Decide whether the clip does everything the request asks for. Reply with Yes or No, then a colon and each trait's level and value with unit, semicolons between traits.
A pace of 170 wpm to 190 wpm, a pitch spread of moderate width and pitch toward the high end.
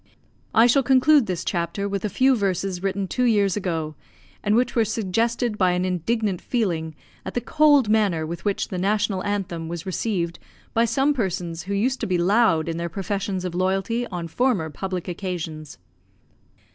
Yes: average, 175 wpm; average, 4.4 semitones; high, 195 Hz